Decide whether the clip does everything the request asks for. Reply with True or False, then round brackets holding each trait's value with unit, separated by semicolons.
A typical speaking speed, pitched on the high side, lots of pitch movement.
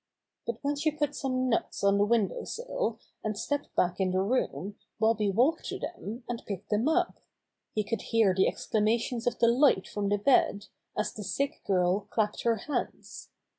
False (180 wpm; 225 Hz; 4.0 semitones)